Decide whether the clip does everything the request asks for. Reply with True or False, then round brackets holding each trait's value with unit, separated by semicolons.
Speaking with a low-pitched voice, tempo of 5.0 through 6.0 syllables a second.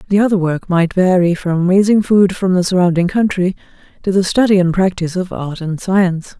False (185 Hz; 5.5 syllables/s)